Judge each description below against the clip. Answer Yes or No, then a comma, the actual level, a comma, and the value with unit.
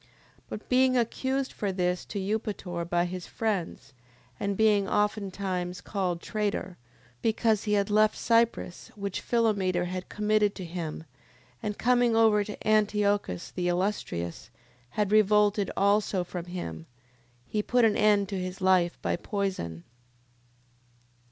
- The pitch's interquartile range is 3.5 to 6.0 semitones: No, average, 2.9 semitones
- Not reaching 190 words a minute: Yes, slow, 135 wpm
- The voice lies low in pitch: No, high, 200 Hz